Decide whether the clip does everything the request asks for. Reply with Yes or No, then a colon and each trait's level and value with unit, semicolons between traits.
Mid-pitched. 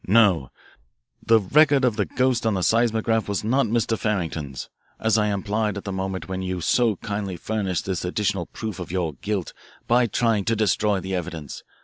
No: low, 105 Hz